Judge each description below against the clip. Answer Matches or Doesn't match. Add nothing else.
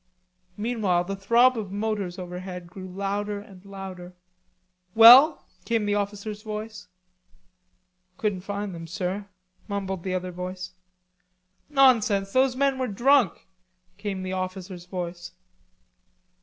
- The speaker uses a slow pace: Matches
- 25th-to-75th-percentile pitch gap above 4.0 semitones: Doesn't match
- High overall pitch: Matches